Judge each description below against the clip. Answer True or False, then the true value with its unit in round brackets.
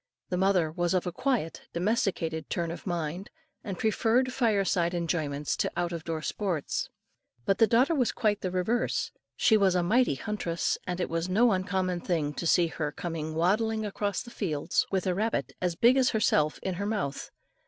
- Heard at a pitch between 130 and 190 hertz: True (185 Hz)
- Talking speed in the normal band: True (190 wpm)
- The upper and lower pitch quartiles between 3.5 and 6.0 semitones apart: True (4.2 semitones)